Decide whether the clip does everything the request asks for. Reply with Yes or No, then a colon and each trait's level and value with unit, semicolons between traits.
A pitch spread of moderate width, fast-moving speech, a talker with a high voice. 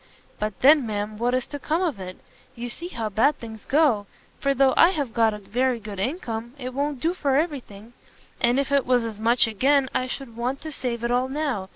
Yes: average, 4.0 semitones; fast, 230 wpm; very high, 250 Hz